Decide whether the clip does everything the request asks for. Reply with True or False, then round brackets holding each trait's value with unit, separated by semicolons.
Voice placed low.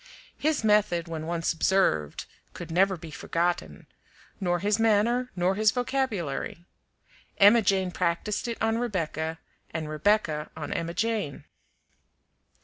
False (185 Hz)